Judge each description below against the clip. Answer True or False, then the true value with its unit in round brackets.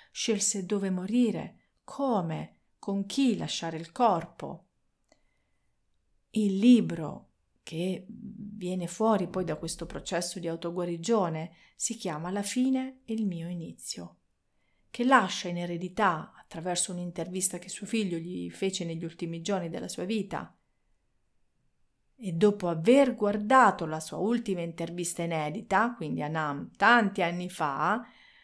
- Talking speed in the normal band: True (125 wpm)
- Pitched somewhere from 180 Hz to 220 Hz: True (185 Hz)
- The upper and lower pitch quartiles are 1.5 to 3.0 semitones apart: False (4.4 semitones)